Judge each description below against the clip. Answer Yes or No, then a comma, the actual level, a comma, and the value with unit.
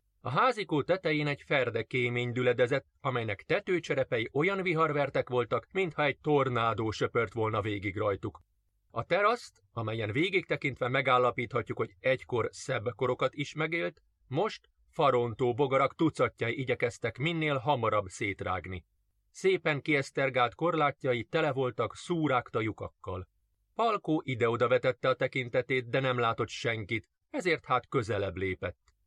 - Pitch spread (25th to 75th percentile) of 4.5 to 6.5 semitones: Yes, wide, 5.5 semitones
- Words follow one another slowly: No, average, 120 wpm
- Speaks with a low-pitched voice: Yes, low, 130 Hz